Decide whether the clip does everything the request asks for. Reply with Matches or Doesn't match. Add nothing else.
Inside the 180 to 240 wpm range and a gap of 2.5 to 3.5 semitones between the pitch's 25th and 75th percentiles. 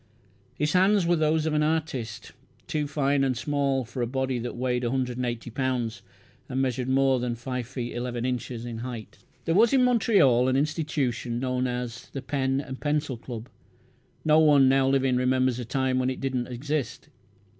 Matches